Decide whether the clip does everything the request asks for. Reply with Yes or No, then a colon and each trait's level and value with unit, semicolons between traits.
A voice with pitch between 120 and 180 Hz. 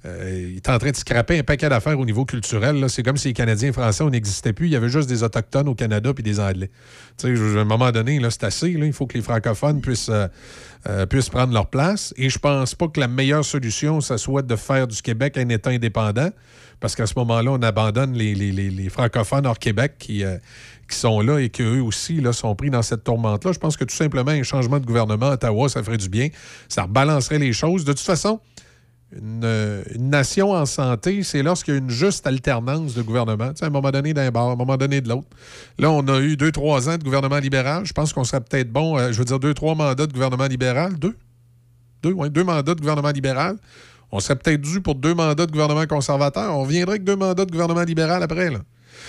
Yes: low, 135 Hz